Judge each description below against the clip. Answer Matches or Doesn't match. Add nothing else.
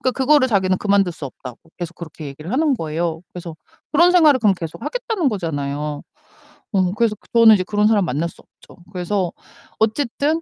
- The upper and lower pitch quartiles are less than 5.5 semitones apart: Doesn't match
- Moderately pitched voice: Doesn't match